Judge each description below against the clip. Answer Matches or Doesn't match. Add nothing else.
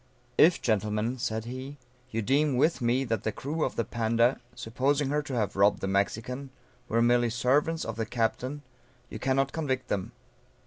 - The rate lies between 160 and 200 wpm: Matches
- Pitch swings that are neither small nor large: Matches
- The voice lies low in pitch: Matches